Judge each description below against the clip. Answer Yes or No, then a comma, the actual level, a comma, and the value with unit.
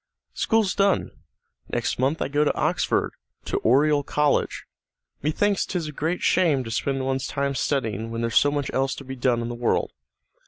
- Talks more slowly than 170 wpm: No, average, 185 wpm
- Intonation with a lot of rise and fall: No, average, 3.0 semitones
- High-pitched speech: No, medium, 140 Hz